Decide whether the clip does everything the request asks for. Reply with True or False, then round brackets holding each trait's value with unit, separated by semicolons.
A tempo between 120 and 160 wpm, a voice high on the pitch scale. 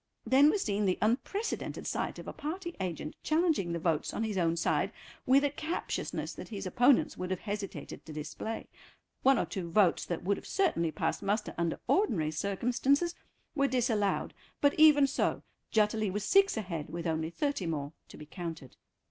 False (180 wpm; 210 Hz)